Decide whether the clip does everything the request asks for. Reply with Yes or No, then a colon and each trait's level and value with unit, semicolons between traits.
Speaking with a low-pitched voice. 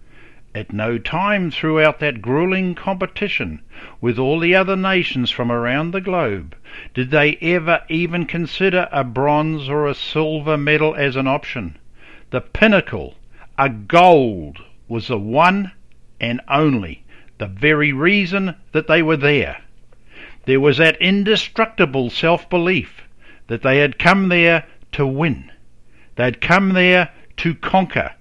No: medium, 155 Hz